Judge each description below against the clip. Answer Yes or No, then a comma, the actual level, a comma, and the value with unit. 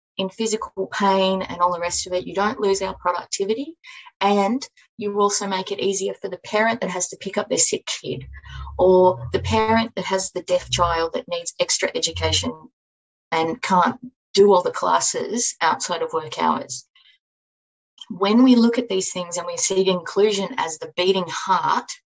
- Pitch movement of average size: Yes, average, 4.4 semitones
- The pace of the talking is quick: No, average, 185 wpm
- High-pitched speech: Yes, high, 195 Hz